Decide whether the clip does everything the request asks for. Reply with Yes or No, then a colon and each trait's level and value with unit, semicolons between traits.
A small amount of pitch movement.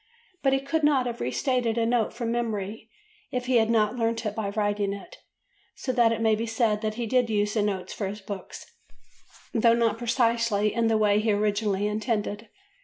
Yes: narrow, 2.2 semitones